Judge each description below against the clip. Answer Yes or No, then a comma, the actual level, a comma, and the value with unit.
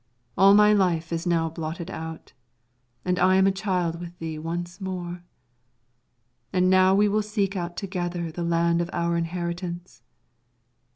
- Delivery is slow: No, average, 155 wpm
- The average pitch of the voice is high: No, medium, 175 Hz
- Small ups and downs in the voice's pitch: Yes, narrow, 2.0 semitones